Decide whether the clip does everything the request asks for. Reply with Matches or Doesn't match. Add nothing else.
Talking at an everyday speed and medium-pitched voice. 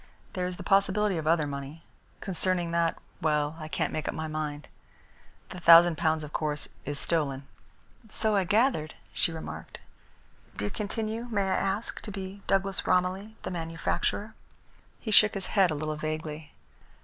Matches